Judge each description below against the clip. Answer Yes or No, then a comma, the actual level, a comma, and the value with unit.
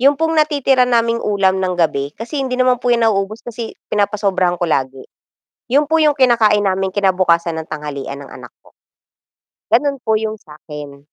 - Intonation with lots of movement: Yes, wide, 6.6 semitones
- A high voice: Yes, high, 210 Hz